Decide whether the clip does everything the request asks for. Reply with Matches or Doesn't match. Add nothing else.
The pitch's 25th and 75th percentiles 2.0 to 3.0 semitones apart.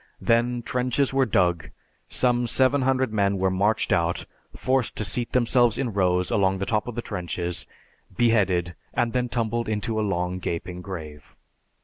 Doesn't match